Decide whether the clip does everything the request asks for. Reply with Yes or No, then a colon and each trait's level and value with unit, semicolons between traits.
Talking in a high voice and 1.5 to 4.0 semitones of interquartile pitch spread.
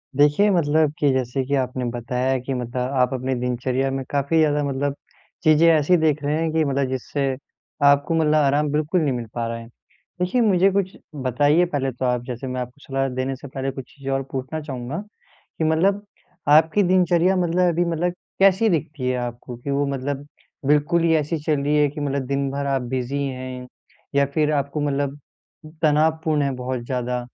No: medium, 140 Hz; average, 3.4 semitones